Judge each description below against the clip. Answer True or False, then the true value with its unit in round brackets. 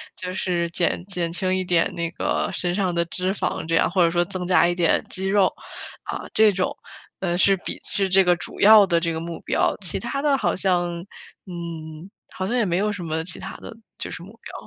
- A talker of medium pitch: True (180 Hz)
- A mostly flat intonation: True (2.1 semitones)